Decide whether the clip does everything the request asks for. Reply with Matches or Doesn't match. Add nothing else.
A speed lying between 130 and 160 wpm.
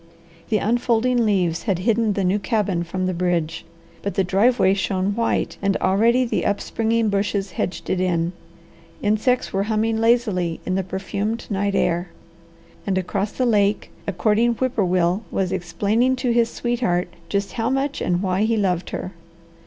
Doesn't match